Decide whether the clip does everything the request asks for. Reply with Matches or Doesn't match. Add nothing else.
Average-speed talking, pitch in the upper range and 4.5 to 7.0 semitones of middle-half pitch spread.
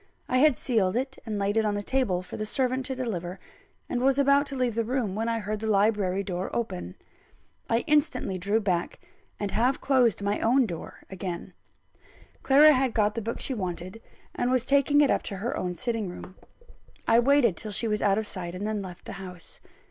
Doesn't match